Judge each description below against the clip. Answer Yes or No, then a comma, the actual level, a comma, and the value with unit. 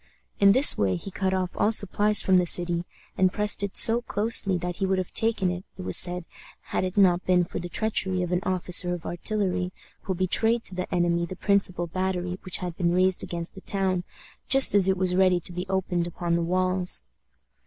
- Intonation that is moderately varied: No, narrow, 1.6 semitones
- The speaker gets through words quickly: Yes, fast, 215 wpm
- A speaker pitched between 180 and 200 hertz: Yes, medium, 185 Hz